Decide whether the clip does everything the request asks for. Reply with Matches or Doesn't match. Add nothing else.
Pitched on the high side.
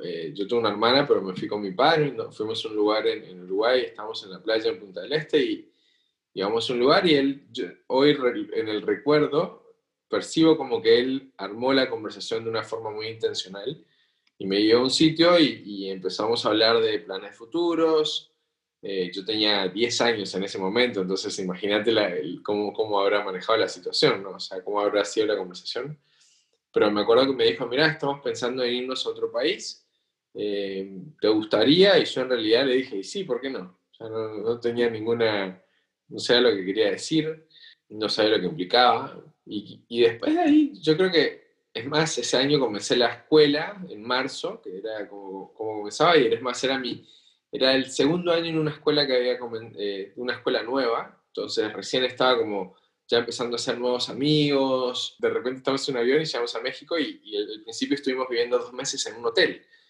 Doesn't match